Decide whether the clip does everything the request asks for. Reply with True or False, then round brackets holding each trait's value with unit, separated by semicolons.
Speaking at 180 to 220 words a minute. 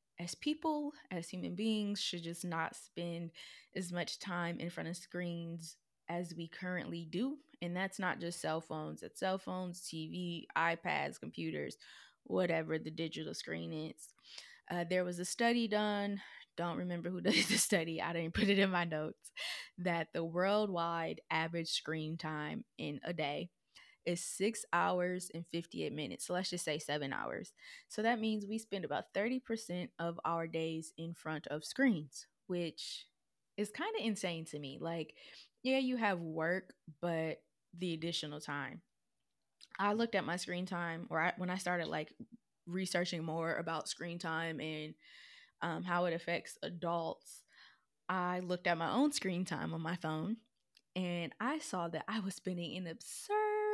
False (165 wpm)